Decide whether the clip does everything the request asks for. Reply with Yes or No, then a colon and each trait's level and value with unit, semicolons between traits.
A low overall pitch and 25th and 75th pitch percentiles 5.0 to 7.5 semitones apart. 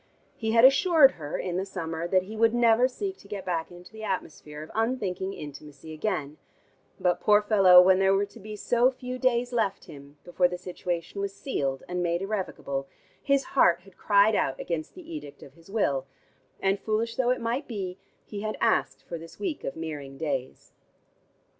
No: high, 195 Hz; wide, 5.5 semitones